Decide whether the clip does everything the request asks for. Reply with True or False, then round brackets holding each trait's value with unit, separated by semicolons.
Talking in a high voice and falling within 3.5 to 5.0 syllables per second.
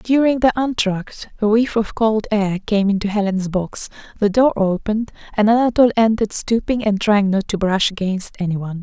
False (210 Hz; 5.4 syllables/s)